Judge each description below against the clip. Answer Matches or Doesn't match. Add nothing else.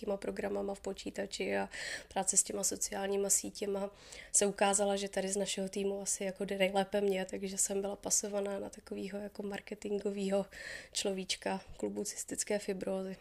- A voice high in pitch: Matches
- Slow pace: Doesn't match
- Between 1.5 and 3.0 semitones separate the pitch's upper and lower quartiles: Doesn't match